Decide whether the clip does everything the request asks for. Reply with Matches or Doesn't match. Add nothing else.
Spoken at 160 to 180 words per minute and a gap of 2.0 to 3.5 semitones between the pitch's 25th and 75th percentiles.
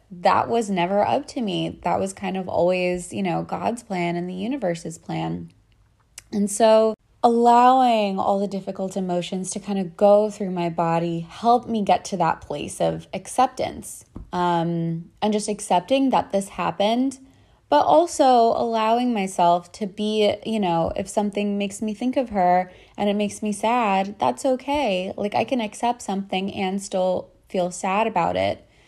Doesn't match